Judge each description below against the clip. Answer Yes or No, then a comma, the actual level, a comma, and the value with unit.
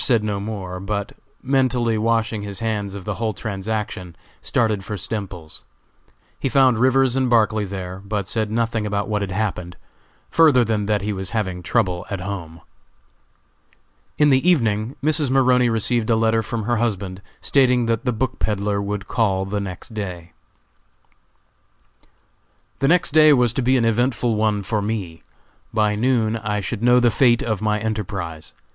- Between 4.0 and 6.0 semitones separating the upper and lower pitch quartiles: No, average, 3.1 semitones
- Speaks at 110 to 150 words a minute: No, average, 165 wpm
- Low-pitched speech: Yes, low, 110 Hz